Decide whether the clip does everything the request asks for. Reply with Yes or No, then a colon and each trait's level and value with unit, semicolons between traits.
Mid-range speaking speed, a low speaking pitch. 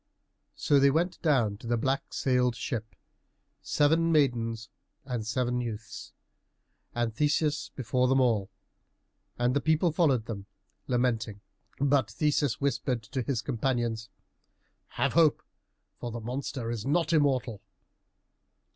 No: slow, 125 wpm; low, 125 Hz